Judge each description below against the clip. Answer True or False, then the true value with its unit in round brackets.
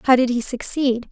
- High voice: True (250 Hz)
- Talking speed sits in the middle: False (215 wpm)